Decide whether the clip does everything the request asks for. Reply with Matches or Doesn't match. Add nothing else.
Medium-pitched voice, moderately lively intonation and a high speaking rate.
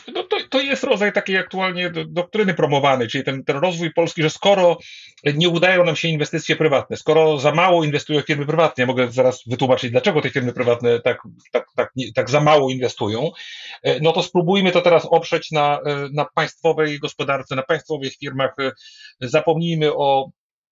Matches